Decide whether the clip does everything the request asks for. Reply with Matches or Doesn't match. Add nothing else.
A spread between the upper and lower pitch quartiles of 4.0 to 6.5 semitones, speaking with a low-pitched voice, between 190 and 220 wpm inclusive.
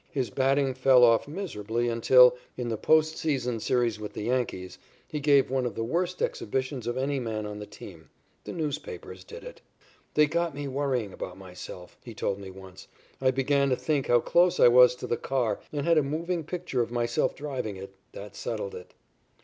Matches